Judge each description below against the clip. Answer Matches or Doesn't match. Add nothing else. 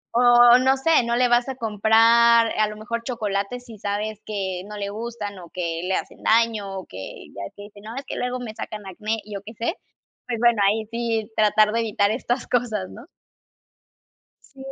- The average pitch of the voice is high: Matches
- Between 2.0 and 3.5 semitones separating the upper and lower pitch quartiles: Matches